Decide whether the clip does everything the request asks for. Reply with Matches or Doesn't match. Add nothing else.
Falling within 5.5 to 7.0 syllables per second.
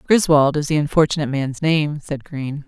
Doesn't match